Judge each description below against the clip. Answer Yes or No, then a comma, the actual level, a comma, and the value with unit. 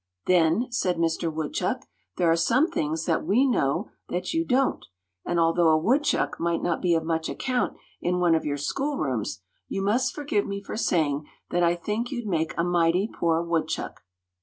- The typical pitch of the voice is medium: Yes, medium, 175 Hz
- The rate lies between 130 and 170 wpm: No, average, 185 wpm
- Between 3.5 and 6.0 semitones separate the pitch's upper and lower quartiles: Yes, average, 4.9 semitones